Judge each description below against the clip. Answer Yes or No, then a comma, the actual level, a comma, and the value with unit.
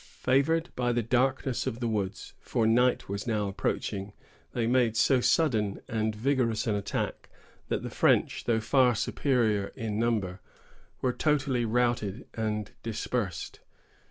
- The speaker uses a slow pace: Yes, slow, 130 wpm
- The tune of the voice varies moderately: Yes, average, 3.0 semitones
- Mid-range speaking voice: No, low, 115 Hz